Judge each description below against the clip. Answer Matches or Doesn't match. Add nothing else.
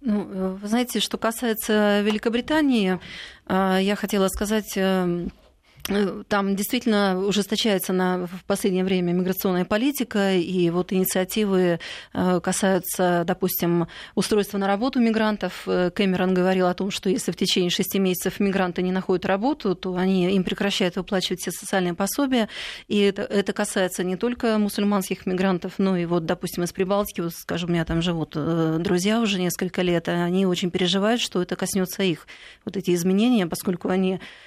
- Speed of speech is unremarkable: Matches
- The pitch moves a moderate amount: Doesn't match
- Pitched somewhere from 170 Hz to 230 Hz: Matches